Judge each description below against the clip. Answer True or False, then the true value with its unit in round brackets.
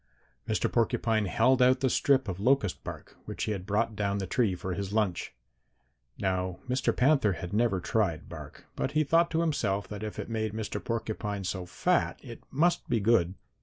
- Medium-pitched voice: False (110 Hz)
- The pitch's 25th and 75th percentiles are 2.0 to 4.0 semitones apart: False (4.5 semitones)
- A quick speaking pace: False (190 wpm)